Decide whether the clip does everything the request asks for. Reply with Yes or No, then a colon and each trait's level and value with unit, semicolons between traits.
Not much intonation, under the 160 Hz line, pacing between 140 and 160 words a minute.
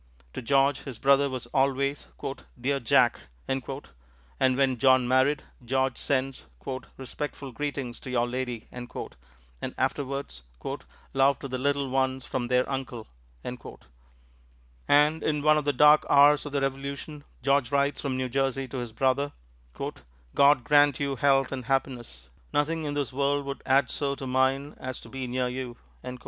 Yes: narrow, 2.0 semitones; low, 135 Hz; average, 155 wpm